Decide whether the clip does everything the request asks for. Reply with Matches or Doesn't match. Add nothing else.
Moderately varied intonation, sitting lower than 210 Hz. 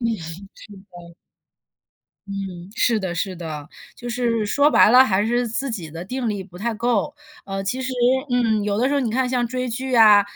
Doesn't match